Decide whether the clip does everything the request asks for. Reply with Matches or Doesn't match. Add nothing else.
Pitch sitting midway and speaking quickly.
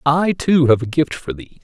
Matches